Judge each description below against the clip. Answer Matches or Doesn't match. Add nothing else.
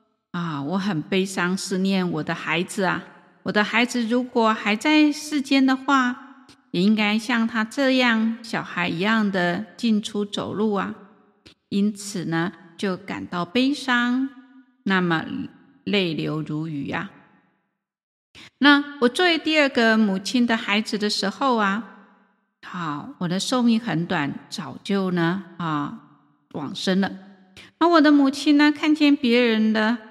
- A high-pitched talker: Matches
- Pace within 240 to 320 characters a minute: Doesn't match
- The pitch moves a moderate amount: Matches